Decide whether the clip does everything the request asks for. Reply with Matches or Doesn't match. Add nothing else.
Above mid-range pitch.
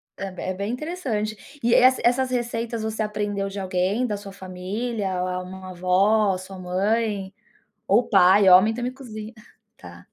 Matches